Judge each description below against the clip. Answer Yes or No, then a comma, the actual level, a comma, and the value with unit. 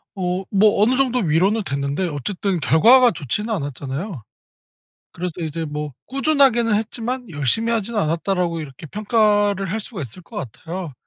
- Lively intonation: Yes, wide, 5.9 semitones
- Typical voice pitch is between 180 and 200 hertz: Yes, high, 190 Hz